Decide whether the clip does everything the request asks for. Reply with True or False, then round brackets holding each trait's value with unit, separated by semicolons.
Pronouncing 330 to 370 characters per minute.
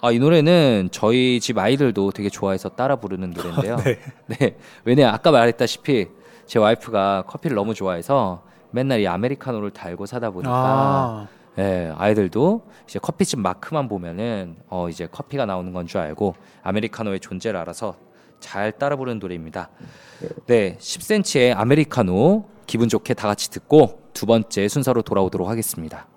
True (355 characters per minute)